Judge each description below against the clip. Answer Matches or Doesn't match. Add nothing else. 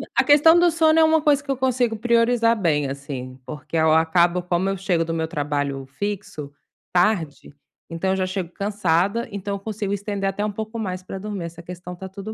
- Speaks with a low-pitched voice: Doesn't match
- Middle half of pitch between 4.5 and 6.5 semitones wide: Matches